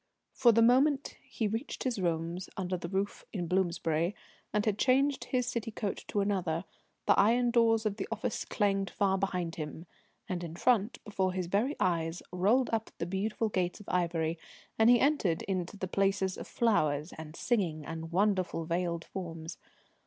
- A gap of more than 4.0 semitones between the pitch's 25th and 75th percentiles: Yes, average, 4.6 semitones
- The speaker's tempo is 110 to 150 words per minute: No, average, 175 wpm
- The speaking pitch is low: No, high, 195 Hz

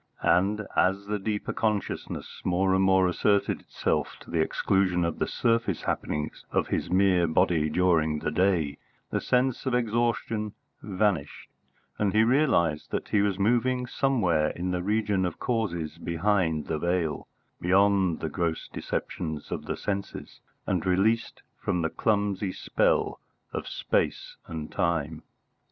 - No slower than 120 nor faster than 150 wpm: Yes, average, 145 wpm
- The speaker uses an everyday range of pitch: Yes, average, 3.9 semitones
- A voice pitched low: Yes, very low, 95 Hz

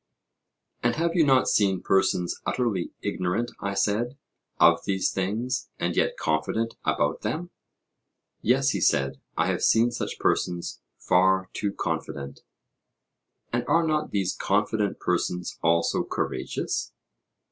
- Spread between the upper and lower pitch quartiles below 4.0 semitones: No, average, 5.1 semitones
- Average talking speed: No, slow, 125 wpm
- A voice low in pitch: Yes, low, 100 Hz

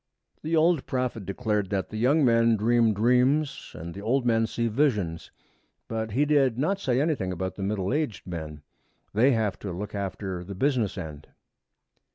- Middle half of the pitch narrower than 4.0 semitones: No, average, 5.1 semitones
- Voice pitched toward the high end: No, low, 110 Hz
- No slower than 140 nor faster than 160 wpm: No, average, 175 wpm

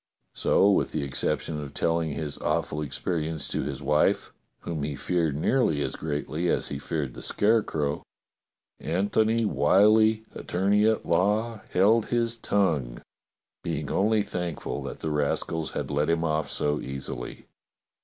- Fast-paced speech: No, average, 145 wpm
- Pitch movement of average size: No, wide, 5.8 semitones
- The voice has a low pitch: Yes, very low, 85 Hz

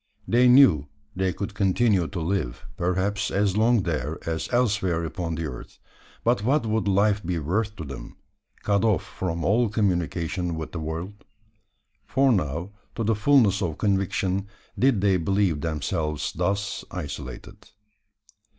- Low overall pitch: Yes, very low, 95 Hz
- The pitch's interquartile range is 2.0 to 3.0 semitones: No, average, 4.2 semitones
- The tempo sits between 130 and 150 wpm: Yes, average, 145 wpm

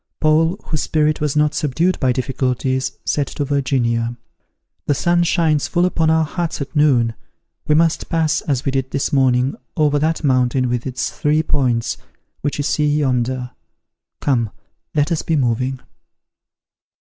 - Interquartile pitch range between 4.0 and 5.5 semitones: No, average, 3.2 semitones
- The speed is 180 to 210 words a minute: No, average, 155 wpm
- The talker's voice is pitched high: No, medium, 145 Hz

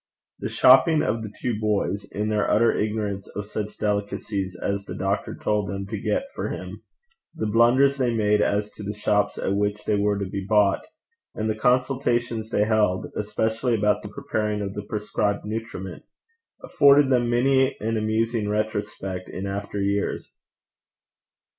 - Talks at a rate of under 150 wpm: No, average, 165 wpm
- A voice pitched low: Yes, low, 105 Hz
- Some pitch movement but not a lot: No, narrow, 1.9 semitones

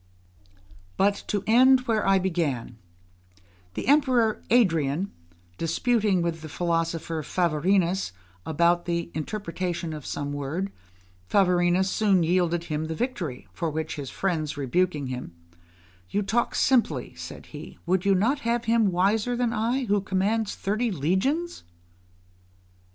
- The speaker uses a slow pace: Yes, slow, 130 wpm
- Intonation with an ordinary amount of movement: Yes, average, 4.9 semitones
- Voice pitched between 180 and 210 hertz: Yes, medium, 185 Hz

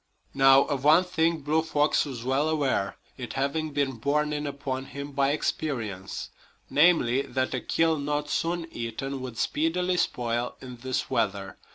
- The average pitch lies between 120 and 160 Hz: Yes, medium, 140 Hz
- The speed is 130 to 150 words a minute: No, average, 160 wpm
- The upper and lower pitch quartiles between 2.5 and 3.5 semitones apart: Yes, average, 3.2 semitones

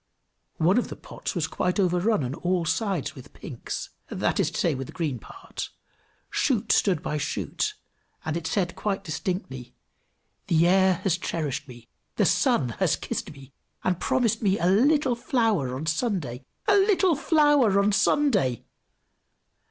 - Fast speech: No, average, 160 wpm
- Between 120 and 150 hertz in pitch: No, medium, 185 Hz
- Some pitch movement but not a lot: No, wide, 7.0 semitones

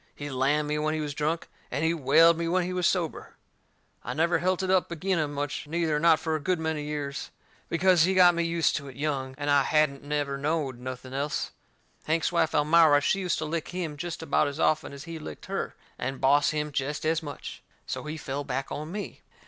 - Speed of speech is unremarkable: No, fast, 225 wpm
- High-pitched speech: No, medium, 155 Hz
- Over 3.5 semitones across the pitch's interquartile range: No, average, 2.7 semitones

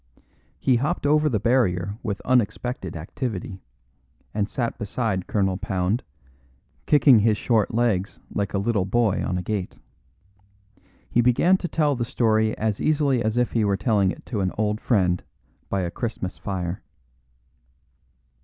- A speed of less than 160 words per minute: Yes, average, 150 wpm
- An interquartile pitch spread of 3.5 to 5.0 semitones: Yes, average, 3.9 semitones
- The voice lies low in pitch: Yes, low, 110 Hz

